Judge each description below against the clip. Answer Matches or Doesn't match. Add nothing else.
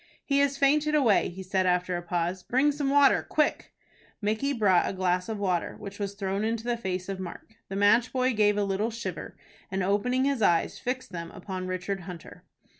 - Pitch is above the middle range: Matches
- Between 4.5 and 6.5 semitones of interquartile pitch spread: Matches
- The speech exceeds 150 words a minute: Matches